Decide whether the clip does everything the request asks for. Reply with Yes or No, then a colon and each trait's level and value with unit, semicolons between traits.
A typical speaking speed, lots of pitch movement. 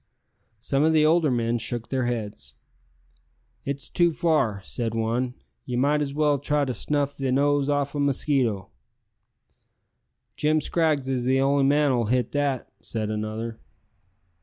No: average, 150 wpm; average, 3.6 semitones